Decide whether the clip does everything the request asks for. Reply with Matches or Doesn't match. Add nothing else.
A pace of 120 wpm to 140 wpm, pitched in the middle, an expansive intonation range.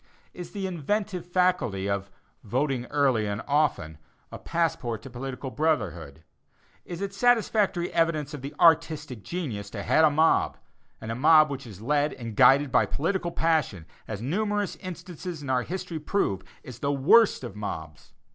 Doesn't match